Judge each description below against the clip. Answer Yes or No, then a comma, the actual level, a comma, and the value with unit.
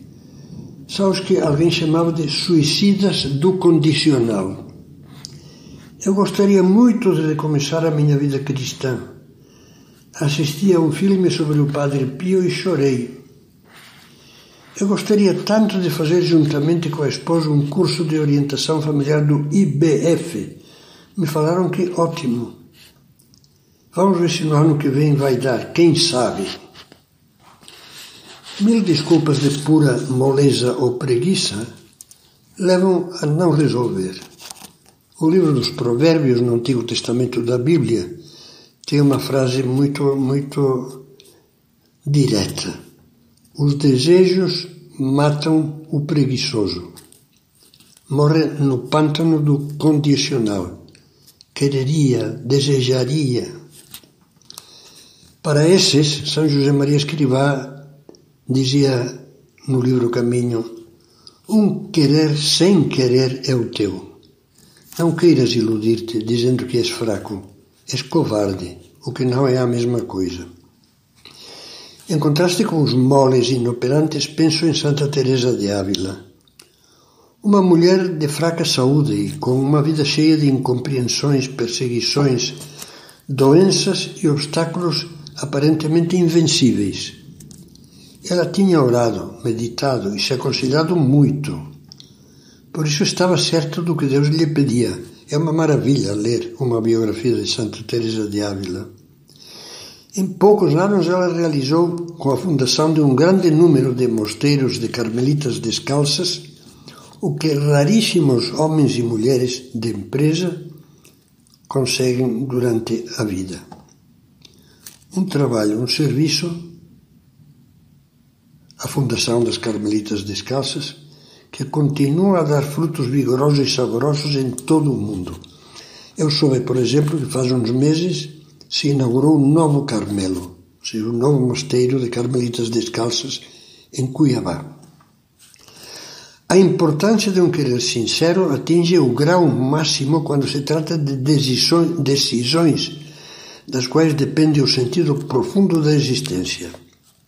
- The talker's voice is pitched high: No, medium, 140 Hz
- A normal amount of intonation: Yes, average, 4.6 semitones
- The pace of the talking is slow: Yes, slow, 115 wpm